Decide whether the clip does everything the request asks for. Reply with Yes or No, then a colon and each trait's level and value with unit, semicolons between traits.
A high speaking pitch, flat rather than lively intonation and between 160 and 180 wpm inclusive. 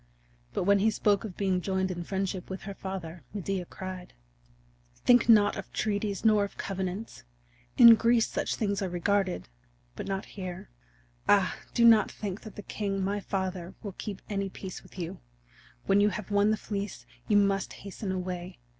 Yes: high, 195 Hz; narrow, 1.7 semitones; average, 170 wpm